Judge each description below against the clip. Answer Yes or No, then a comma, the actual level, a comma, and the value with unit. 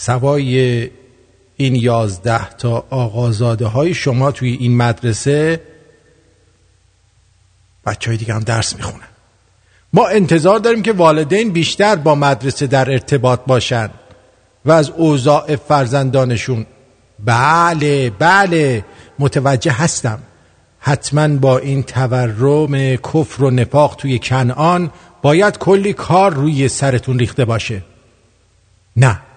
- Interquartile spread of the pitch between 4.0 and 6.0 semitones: Yes, average, 4.3 semitones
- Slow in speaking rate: Yes, slow, 105 wpm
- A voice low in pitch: Yes, low, 130 Hz